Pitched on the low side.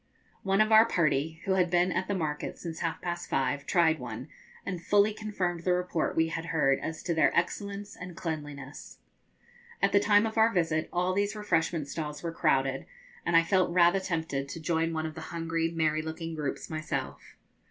No: medium, 165 Hz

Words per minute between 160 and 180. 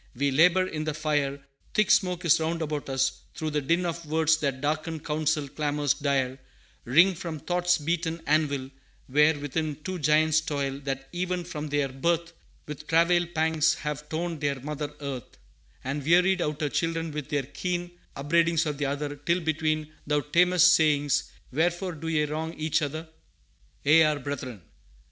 Yes: average, 165 wpm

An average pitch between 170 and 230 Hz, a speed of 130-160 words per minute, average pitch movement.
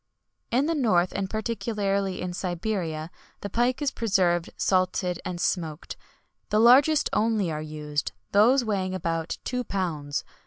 Yes: high, 190 Hz; average, 140 wpm; average, 4.6 semitones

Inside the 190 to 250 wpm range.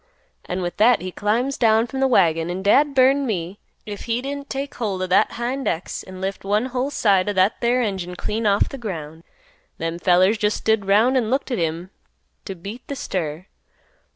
Yes: fast, 205 wpm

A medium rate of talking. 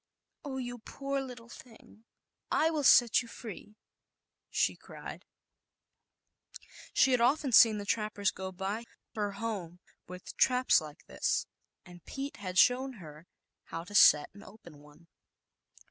No: slow, 125 wpm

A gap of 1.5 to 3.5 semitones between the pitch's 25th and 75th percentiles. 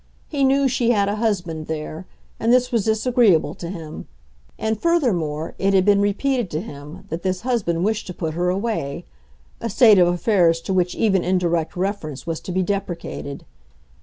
No: average, 5.0 semitones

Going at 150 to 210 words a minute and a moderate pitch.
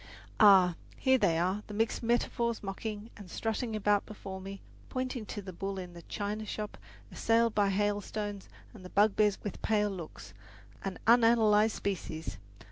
No: average, 155 wpm; high, 205 Hz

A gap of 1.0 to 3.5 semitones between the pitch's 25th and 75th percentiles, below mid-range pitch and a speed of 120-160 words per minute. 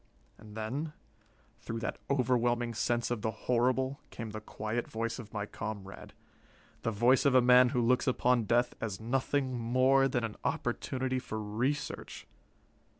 Yes: narrow, 2.6 semitones; low, 120 Hz; average, 150 wpm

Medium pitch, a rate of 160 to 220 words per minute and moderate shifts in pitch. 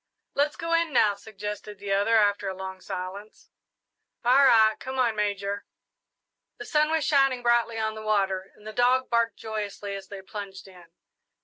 No: high, 215 Hz; average, 175 wpm; average, 3.6 semitones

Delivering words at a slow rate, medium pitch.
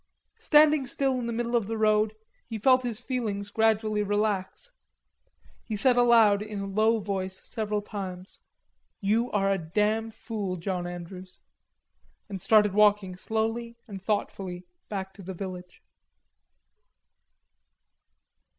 No: slow, 130 wpm; high, 210 Hz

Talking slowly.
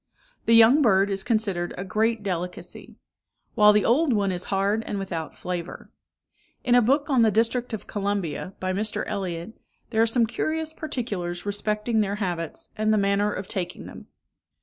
No: average, 170 wpm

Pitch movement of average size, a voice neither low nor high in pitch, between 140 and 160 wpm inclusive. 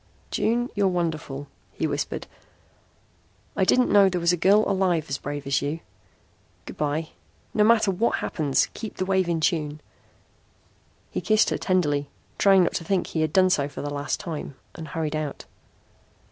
No: average, 4.5 semitones; medium, 170 Hz; average, 175 wpm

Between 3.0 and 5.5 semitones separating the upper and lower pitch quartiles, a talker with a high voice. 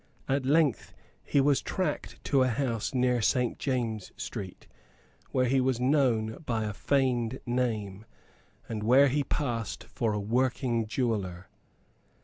No: average, 3.3 semitones; low, 125 Hz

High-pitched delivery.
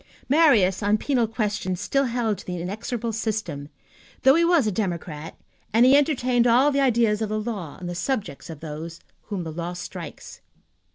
Yes: high, 215 Hz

